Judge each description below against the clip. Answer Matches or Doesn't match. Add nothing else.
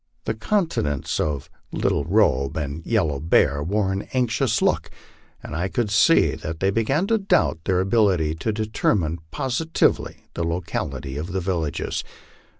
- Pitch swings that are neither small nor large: Doesn't match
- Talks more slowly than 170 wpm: Matches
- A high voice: Doesn't match